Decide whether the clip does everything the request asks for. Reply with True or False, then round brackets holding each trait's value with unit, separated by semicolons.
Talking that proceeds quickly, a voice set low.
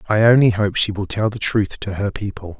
True (255 wpm; 105 Hz)